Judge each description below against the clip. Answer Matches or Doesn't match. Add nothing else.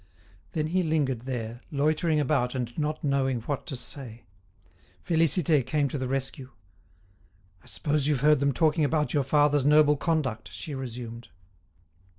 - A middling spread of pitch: Matches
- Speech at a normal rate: Matches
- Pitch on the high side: Doesn't match